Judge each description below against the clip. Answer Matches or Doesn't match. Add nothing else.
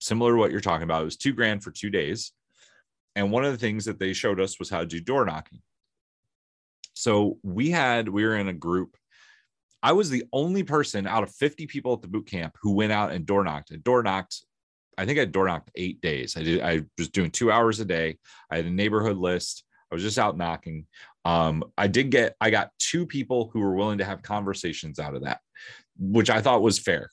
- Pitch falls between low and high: Doesn't match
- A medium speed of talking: Doesn't match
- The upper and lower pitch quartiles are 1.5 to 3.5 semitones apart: Doesn't match